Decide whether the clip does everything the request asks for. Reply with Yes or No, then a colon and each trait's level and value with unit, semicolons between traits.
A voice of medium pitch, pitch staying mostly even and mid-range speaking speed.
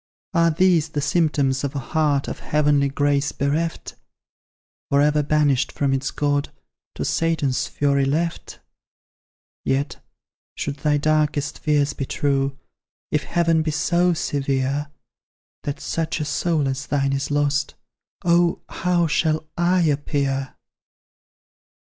No: medium, 145 Hz; narrow, 2.3 semitones; slow, 125 wpm